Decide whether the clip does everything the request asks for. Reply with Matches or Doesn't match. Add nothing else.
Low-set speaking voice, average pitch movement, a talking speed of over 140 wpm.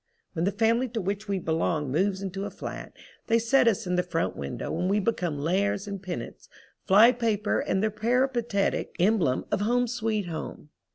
Doesn't match